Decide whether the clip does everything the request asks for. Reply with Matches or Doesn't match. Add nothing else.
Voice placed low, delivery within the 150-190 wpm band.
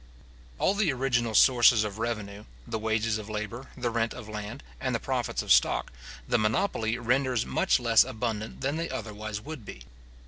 Matches